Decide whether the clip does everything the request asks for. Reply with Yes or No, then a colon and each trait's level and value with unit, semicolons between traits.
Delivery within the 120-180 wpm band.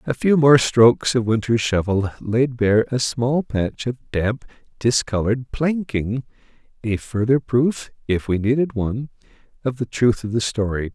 Yes: average, 160 wpm